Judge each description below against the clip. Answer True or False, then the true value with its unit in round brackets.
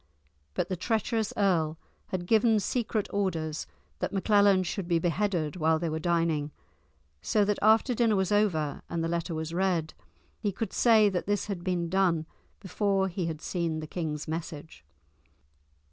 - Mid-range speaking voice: True (180 Hz)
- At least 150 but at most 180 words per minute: True (160 wpm)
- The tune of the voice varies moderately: True (3.9 semitones)